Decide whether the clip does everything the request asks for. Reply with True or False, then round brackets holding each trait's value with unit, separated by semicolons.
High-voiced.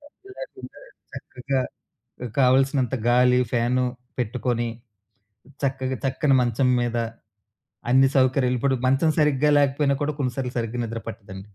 False (130 Hz)